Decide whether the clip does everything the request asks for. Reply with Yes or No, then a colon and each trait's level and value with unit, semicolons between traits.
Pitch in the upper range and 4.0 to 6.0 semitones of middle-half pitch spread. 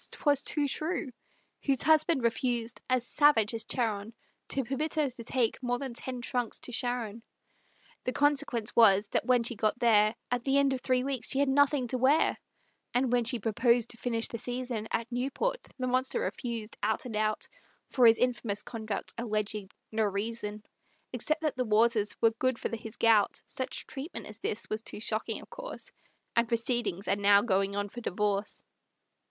No: high, 235 Hz; average, 3.0 semitones